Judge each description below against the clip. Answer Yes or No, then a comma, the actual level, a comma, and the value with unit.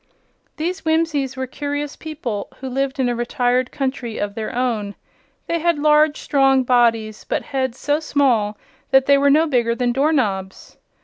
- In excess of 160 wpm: Yes, average, 170 wpm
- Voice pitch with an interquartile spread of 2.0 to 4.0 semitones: Yes, average, 3.5 semitones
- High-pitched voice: Yes, very high, 265 Hz